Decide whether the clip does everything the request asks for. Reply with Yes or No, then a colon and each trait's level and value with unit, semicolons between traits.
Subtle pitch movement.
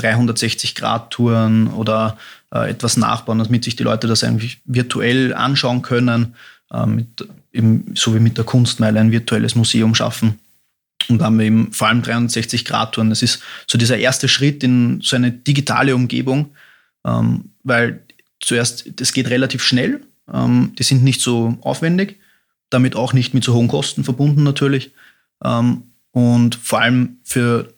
Yes: narrow, 2.3 semitones